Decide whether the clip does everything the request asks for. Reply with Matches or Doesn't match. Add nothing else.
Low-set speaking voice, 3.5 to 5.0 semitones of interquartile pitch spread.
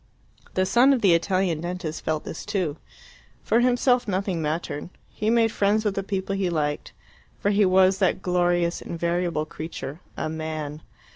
Doesn't match